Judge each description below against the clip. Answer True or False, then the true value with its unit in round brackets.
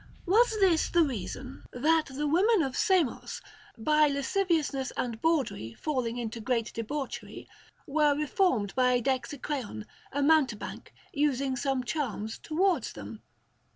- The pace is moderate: False (120 wpm)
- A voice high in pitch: True (275 Hz)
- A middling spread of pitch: True (4.3 semitones)